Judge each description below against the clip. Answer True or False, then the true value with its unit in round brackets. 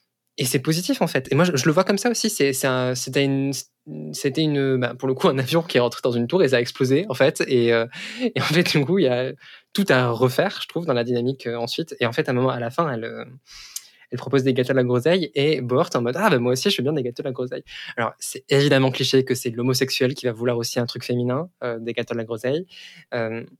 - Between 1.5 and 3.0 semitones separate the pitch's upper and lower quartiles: True (2.7 semitones)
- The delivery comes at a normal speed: False (300 wpm)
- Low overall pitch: True (130 Hz)